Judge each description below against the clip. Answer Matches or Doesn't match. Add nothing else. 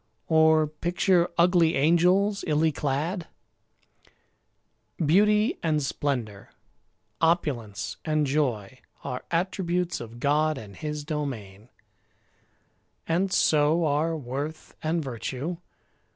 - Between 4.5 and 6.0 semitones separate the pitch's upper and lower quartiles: Doesn't match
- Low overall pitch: Doesn't match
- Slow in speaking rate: Matches